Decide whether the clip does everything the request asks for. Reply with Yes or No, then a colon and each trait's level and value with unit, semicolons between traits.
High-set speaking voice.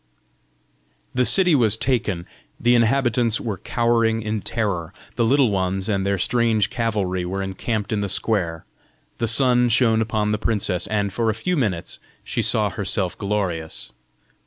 No: low, 110 Hz